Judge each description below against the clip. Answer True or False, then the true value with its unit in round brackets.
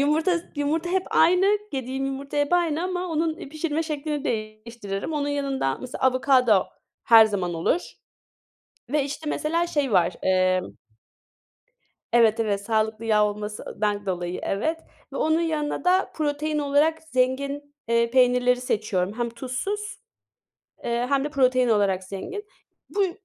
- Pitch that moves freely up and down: True (6.2 semitones)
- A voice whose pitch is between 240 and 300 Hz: True (265 Hz)